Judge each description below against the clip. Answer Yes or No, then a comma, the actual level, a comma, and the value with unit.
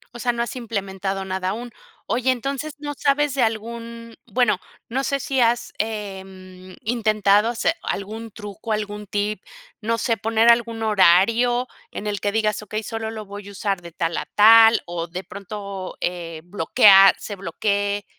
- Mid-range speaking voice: No, high, 215 Hz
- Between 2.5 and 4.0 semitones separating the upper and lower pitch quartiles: Yes, average, 3.0 semitones